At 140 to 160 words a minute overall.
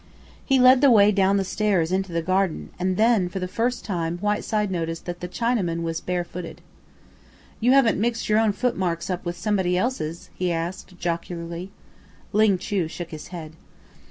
No: average, 180 wpm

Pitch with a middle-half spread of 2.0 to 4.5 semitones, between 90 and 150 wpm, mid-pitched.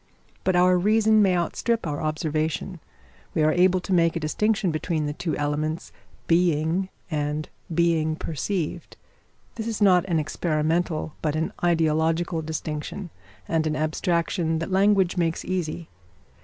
Yes: average, 2.7 semitones; average, 140 wpm; medium, 165 Hz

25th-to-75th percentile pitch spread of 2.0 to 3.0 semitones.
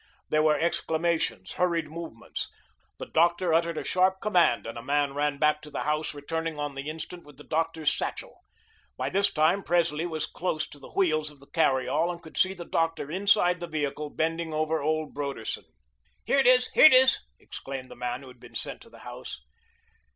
Yes: average, 2.7 semitones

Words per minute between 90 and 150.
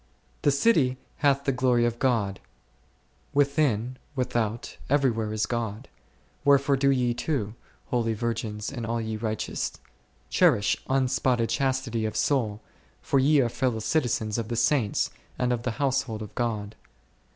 Yes: average, 145 wpm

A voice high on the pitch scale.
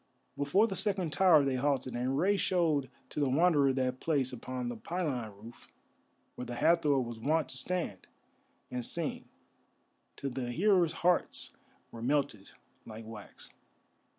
No: medium, 140 Hz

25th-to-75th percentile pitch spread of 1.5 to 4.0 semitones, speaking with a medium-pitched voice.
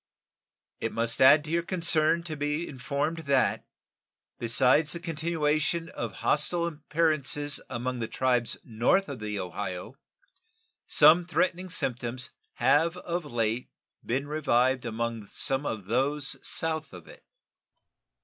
No: average, 5.1 semitones; medium, 145 Hz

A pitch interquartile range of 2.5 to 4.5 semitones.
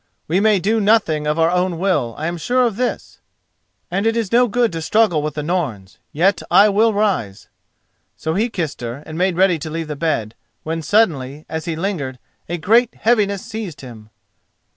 No: wide, 5.6 semitones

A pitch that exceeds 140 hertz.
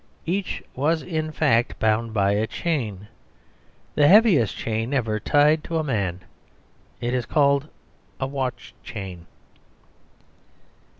No: low, 130 Hz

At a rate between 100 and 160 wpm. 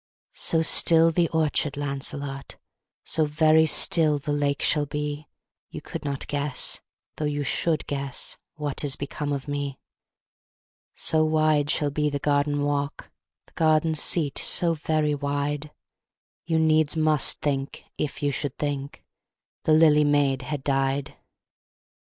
Yes: average, 140 wpm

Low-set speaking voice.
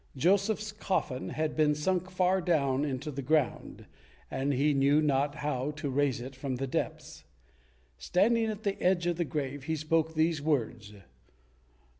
No: medium, 150 Hz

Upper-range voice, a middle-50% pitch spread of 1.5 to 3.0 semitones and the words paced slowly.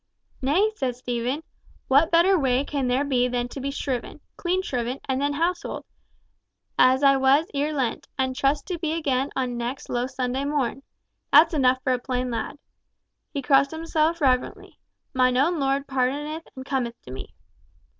No: very high, 270 Hz; average, 2.7 semitones; average, 165 wpm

